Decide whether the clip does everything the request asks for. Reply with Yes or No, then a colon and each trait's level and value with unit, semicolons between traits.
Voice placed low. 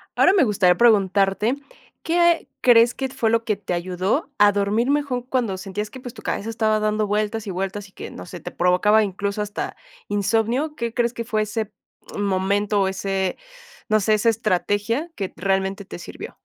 No: high, 210 Hz